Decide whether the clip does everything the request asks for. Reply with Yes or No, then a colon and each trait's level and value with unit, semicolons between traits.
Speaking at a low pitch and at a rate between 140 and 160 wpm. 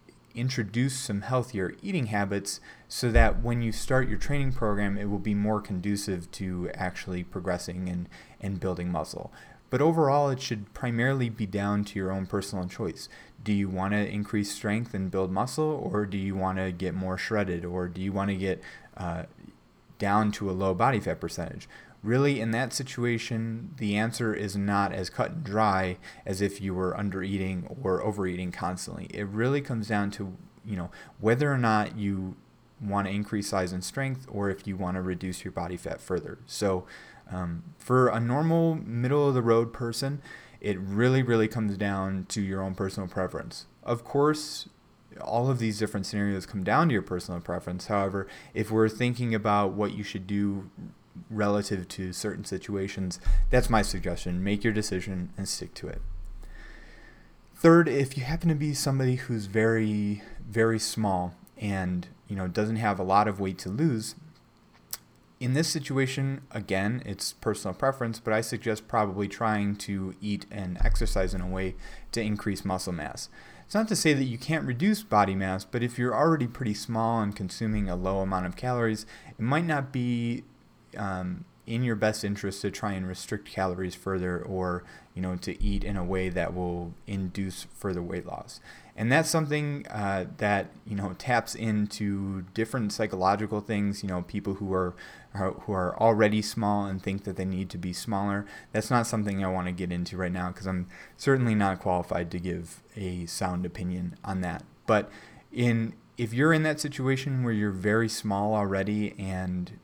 No: low, 100 Hz; average, 180 wpm